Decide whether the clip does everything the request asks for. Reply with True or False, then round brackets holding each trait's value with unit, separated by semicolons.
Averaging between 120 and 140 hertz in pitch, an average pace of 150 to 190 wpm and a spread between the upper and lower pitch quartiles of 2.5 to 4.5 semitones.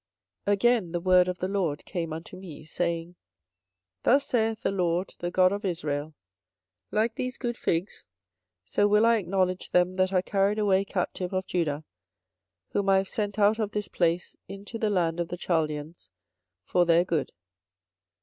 False (185 Hz; 175 wpm; 3.2 semitones)